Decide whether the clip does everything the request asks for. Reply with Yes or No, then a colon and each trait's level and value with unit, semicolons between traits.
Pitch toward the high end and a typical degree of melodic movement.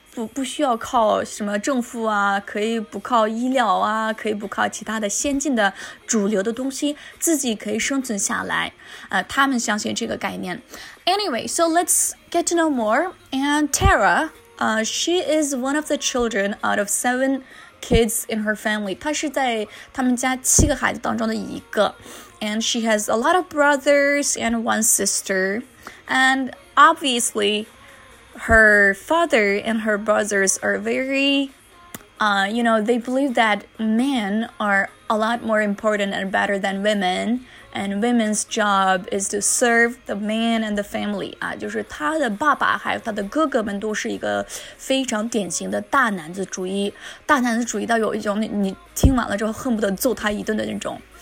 Yes: high, 225 Hz; average, 4.4 semitones